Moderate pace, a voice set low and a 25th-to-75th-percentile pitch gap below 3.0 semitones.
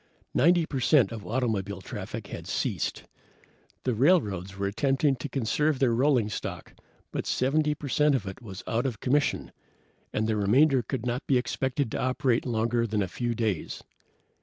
No: average, 160 wpm; low, 125 Hz; average, 4.1 semitones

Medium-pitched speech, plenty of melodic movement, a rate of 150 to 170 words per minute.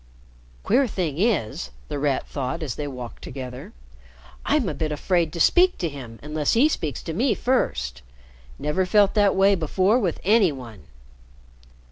Yes: medium, 165 Hz; wide, 6.9 semitones; average, 160 wpm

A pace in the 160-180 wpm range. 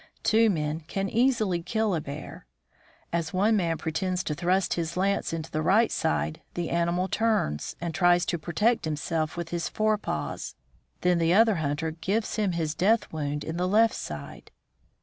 Yes: average, 175 wpm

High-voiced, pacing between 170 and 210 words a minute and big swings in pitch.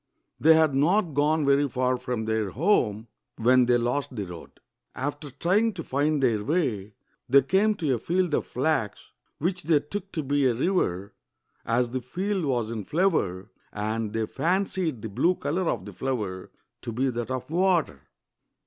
No: low, 135 Hz; average, 175 wpm; wide, 6.3 semitones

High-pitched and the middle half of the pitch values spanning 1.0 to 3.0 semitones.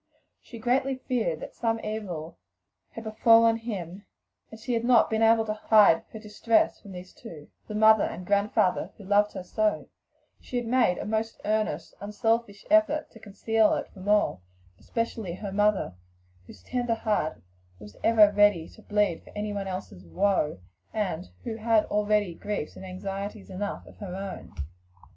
Yes: high, 210 Hz; average, 2.7 semitones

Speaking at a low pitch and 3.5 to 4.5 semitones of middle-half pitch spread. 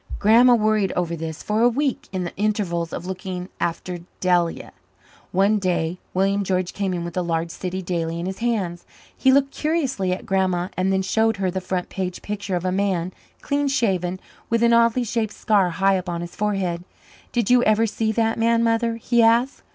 No: high, 195 Hz; average, 4.1 semitones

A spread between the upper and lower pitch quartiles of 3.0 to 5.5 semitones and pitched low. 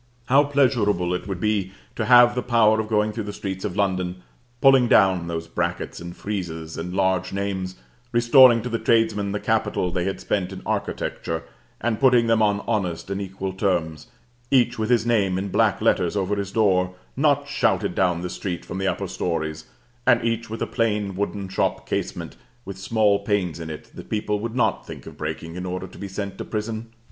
Yes: average, 3.6 semitones; low, 100 Hz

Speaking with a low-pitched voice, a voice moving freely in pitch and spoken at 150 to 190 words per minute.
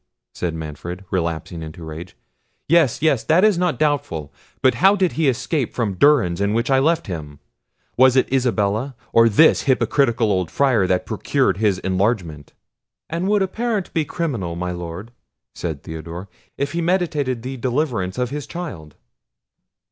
Yes: low, 120 Hz; wide, 8.8 semitones; average, 160 wpm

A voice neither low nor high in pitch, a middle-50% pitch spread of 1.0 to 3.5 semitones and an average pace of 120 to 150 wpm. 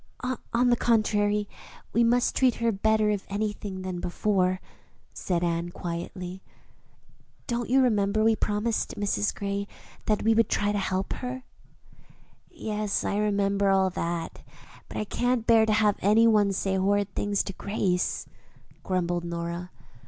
No: high, 205 Hz; average, 2.7 semitones; average, 145 wpm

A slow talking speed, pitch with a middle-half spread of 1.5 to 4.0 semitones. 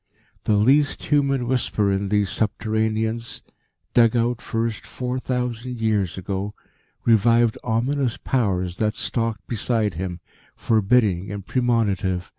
Yes: slow, 115 wpm; average, 3.3 semitones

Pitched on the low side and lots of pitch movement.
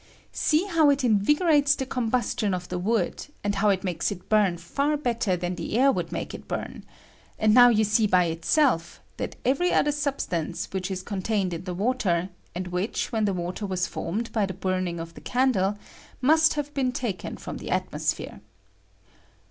No: high, 210 Hz; wide, 6.0 semitones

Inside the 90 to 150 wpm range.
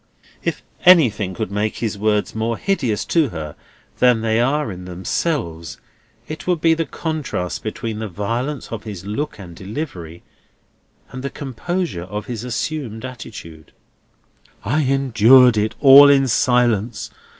Yes: average, 140 wpm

